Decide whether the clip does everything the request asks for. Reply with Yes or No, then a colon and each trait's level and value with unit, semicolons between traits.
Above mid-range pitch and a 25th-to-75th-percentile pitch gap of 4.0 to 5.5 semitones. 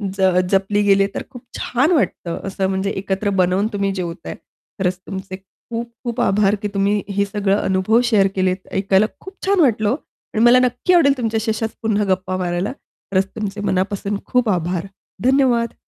No: high, 200 Hz; average, 3.5 semitones